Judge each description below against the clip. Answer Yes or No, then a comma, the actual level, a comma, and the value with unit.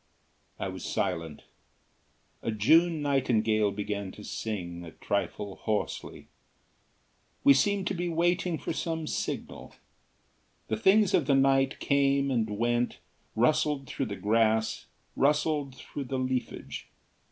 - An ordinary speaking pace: No, slow, 125 wpm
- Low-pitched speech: Yes, low, 130 Hz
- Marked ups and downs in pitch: Yes, wide, 5.7 semitones